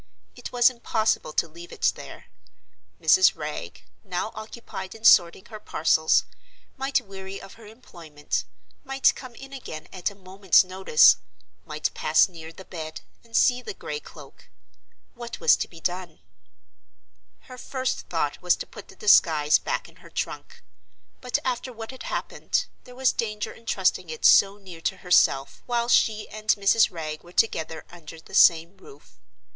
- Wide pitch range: Yes, wide, 6.1 semitones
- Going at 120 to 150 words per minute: No, average, 165 wpm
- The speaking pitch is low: No, high, 195 Hz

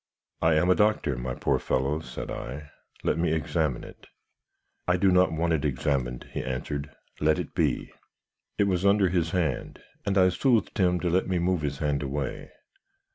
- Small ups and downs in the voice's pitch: No, average, 4.4 semitones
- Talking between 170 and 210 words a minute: Yes, average, 185 wpm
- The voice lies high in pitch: No, very low, 80 Hz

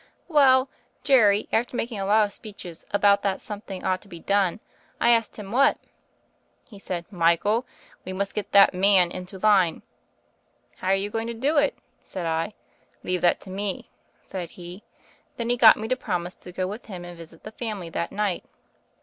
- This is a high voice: Yes, high, 200 Hz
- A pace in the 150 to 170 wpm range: No, average, 190 wpm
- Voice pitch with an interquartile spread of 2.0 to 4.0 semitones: Yes, average, 3.4 semitones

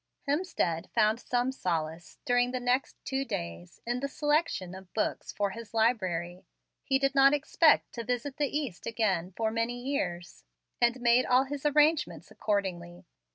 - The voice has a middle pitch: No, high, 240 Hz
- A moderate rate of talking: Yes, average, 155 wpm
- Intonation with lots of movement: Yes, wide, 6.4 semitones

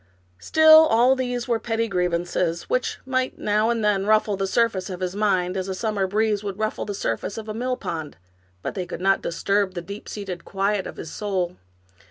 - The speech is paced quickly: Yes, fast, 210 wpm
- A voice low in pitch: No, high, 205 Hz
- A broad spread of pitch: No, average, 3.2 semitones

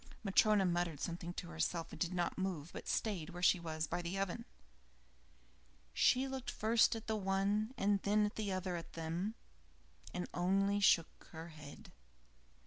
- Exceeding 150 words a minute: Yes, average, 165 wpm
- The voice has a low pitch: No, high, 190 Hz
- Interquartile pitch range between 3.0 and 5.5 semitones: Yes, average, 3.4 semitones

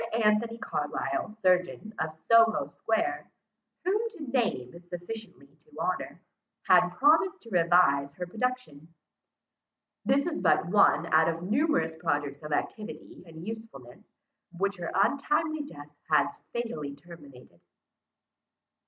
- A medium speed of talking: No, slow, 120 wpm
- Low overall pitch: No, medium, 180 Hz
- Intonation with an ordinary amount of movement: No, wide, 6.6 semitones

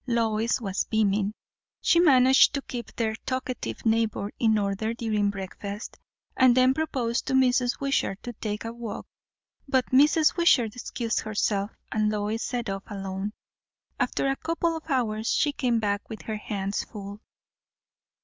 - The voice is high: Yes, high, 225 Hz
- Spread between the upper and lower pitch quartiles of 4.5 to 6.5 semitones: No, average, 3.7 semitones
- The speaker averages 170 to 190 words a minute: No, average, 150 wpm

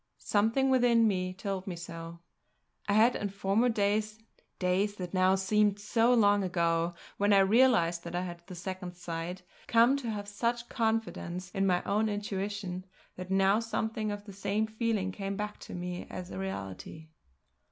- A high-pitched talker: Yes, high, 200 Hz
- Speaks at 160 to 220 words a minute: Yes, average, 170 wpm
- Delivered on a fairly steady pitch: No, average, 3.0 semitones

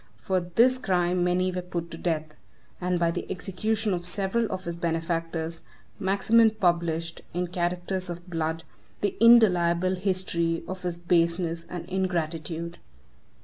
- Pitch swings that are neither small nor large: No, narrow, 1.9 semitones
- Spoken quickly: No, average, 140 wpm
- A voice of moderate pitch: Yes, medium, 175 Hz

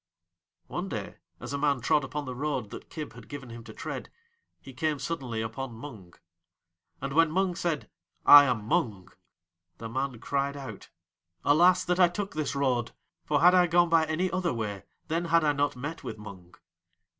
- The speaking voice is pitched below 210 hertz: Yes, medium, 140 Hz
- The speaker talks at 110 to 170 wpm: No, average, 185 wpm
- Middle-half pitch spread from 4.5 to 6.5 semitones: Yes, average, 5.3 semitones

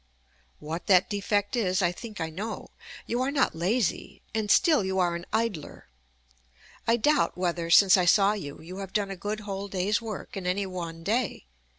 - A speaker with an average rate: Yes, average, 190 wpm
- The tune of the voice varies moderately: Yes, average, 3.2 semitones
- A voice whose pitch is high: Yes, high, 195 Hz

